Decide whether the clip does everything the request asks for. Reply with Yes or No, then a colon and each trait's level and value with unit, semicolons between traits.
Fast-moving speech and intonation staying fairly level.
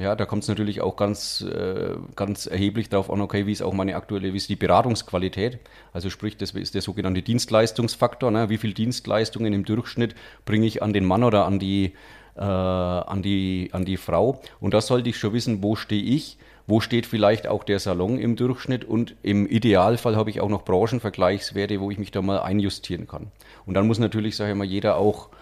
Yes: fast, 210 wpm; narrow, 2.3 semitones